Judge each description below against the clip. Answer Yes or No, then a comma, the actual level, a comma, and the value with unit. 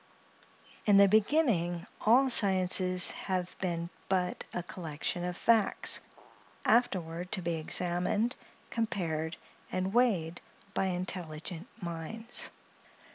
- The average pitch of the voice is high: No, medium, 180 Hz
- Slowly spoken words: Yes, slow, 100 wpm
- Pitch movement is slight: No, average, 3.2 semitones